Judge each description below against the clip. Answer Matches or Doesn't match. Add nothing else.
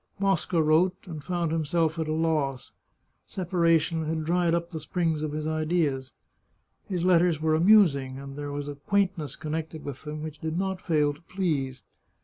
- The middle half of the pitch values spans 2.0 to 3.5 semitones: Matches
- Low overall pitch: Doesn't match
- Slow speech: Doesn't match